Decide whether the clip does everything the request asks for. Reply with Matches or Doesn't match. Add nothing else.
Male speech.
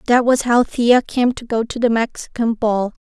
Doesn't match